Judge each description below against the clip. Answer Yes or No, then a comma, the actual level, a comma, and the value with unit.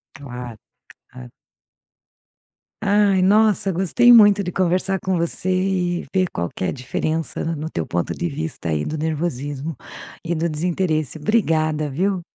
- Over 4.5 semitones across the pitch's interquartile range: No, average, 4.2 semitones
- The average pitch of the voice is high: No, medium, 165 Hz